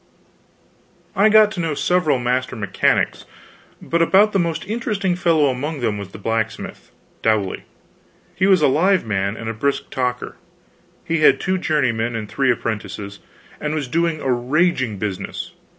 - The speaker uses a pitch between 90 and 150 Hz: Yes, low, 135 Hz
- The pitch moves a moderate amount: No, wide, 7.3 semitones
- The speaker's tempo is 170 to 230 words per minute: No, average, 155 wpm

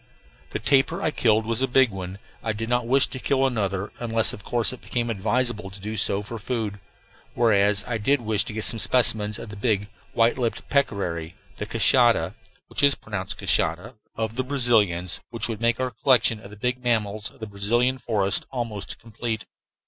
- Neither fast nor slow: Yes, average, 185 wpm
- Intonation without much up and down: No, average, 3.0 semitones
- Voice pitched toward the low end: Yes, low, 110 Hz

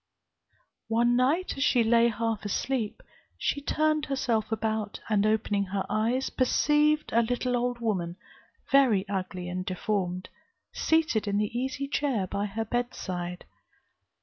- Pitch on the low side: No, high, 225 Hz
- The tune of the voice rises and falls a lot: No, average, 4.2 semitones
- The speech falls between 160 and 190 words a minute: No, slow, 135 wpm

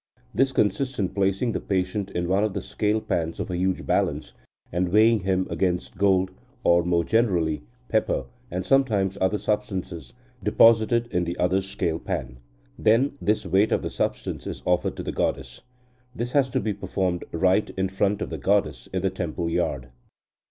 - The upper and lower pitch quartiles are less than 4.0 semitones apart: Yes, average, 3.2 semitones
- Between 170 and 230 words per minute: Yes, average, 180 wpm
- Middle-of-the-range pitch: No, very low, 95 Hz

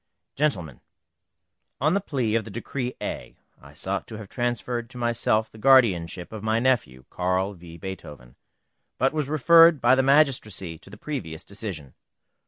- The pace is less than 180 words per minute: Yes, average, 160 wpm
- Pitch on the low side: Yes, low, 110 Hz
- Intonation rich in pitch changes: Yes, wide, 6.5 semitones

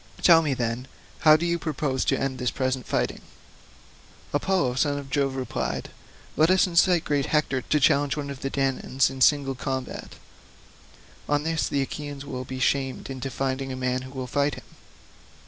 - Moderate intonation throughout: No, narrow, 2.2 semitones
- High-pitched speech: No, low, 135 Hz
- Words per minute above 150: Yes, average, 180 wpm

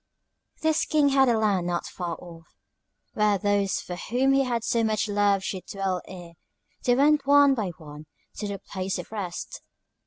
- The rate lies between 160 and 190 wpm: Yes, average, 180 wpm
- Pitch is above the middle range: Yes, high, 205 Hz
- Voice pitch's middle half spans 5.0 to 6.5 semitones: Yes, average, 5.3 semitones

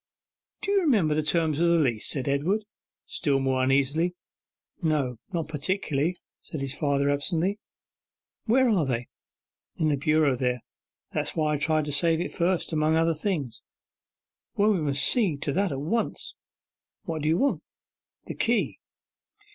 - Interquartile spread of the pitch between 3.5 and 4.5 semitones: Yes, average, 3.8 semitones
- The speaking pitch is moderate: Yes, medium, 155 Hz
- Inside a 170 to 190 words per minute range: No, average, 160 wpm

